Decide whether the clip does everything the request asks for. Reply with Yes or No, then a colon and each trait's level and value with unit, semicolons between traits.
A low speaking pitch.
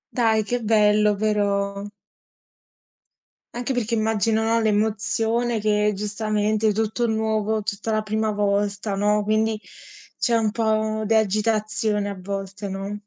No: high, 215 Hz